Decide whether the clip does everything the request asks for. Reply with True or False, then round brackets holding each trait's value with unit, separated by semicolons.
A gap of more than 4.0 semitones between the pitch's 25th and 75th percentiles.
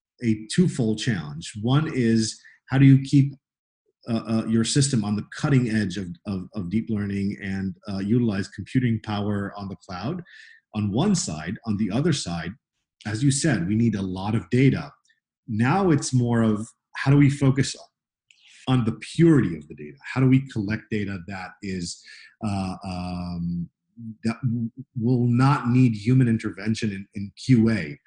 True (4.6 semitones)